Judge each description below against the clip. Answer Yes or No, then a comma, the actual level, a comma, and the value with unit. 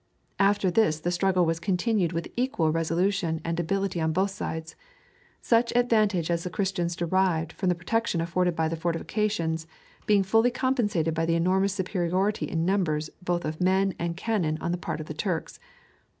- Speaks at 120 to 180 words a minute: Yes, average, 175 wpm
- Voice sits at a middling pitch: Yes, medium, 180 Hz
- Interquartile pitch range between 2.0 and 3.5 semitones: Yes, average, 3.2 semitones